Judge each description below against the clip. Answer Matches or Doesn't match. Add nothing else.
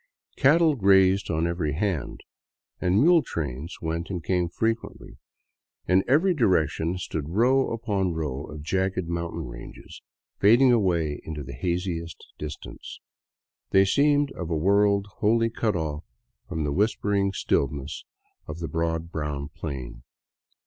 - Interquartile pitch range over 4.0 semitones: Matches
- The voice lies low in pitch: Matches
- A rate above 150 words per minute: Doesn't match